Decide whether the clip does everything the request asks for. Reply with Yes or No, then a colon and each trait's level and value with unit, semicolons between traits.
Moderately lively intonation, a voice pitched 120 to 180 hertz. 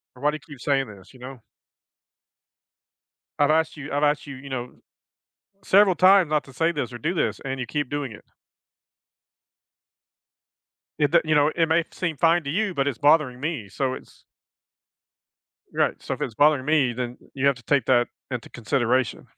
Yes: average, 3.4 semitones; medium, 140 Hz